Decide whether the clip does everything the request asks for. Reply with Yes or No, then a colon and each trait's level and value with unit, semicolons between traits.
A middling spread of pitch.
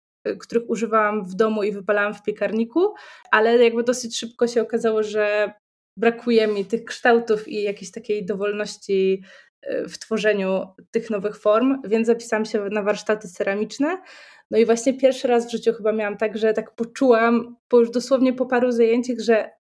No: narrow, 2.0 semitones